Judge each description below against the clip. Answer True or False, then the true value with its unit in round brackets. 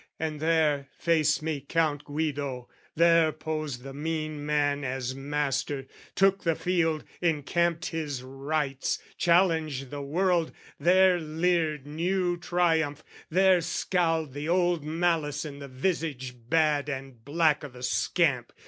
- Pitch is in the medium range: True (155 Hz)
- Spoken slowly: True (130 wpm)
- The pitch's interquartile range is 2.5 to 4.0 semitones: True (2.9 semitones)